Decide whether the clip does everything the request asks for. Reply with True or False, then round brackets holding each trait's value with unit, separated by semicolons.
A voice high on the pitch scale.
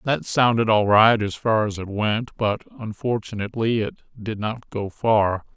False (110 Hz)